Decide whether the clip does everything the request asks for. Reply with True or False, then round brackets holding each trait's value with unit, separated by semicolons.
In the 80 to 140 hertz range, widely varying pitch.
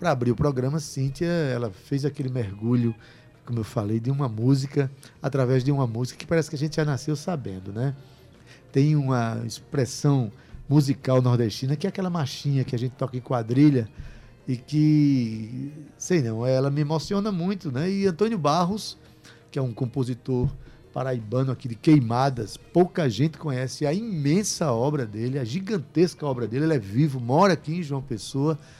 False (135 Hz; 3.7 semitones)